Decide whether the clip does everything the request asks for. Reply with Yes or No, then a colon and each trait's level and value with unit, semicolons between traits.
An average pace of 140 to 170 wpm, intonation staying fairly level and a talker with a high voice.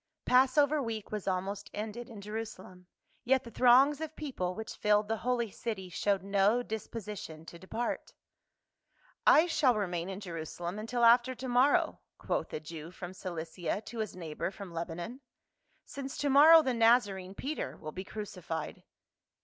No: average, 160 wpm; average, 5.1 semitones; high, 210 Hz